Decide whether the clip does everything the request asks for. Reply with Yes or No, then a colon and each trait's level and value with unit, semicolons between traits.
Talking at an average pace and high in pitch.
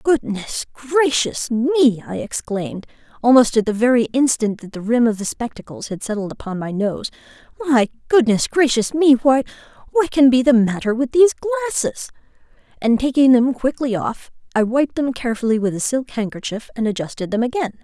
Yes: average, 165 wpm; high, 240 Hz